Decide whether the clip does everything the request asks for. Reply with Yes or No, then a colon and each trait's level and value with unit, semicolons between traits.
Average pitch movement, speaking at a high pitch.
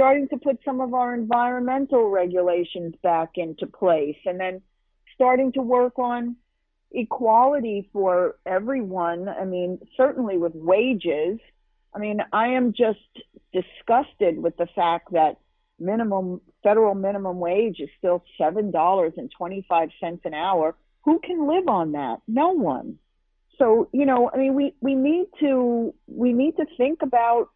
No: wide, 6.3 semitones; high, 220 Hz